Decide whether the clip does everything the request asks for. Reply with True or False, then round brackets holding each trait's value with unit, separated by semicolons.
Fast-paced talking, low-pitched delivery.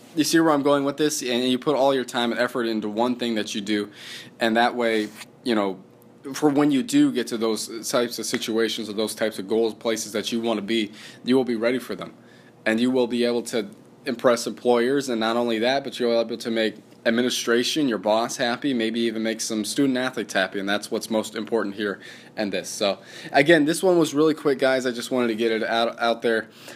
True (245 wpm; 115 Hz)